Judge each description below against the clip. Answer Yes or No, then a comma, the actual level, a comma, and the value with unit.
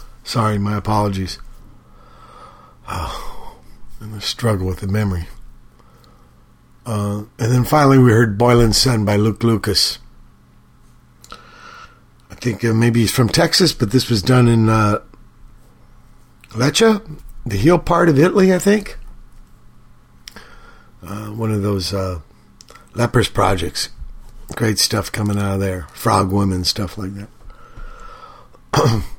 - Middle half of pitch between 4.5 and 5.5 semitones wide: No, average, 3.6 semitones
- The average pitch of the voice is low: Yes, low, 110 Hz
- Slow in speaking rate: Yes, slow, 125 wpm